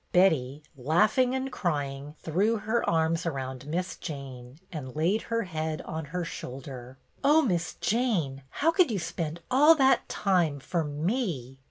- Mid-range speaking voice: Yes, medium, 165 Hz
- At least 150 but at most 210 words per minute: Yes, average, 155 wpm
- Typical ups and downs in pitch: No, wide, 7.2 semitones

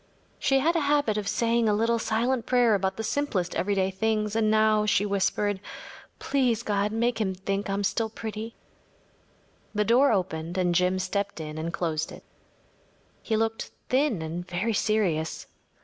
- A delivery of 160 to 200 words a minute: Yes, average, 165 wpm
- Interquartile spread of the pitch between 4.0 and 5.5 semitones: No, average, 3.3 semitones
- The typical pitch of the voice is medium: No, high, 210 Hz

